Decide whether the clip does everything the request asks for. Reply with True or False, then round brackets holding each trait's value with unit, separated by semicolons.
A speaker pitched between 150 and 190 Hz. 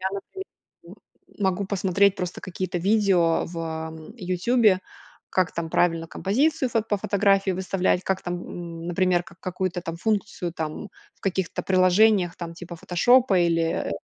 True (185 Hz)